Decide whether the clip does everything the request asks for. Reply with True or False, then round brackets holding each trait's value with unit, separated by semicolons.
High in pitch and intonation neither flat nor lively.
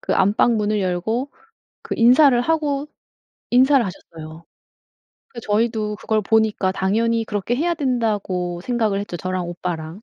True (215 Hz; 4.5 semitones)